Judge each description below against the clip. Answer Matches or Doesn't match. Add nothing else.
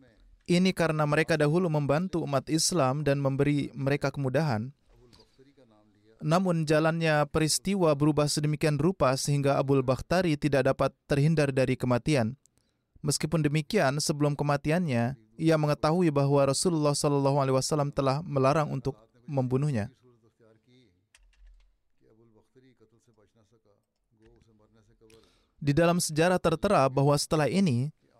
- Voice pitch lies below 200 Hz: Matches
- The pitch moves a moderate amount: Matches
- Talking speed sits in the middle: Matches